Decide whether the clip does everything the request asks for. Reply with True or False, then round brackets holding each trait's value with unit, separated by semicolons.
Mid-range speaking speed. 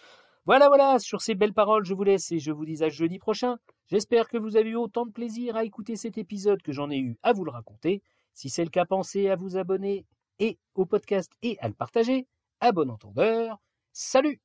False (230 wpm)